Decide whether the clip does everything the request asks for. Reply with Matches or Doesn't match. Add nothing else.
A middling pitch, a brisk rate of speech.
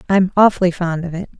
Matches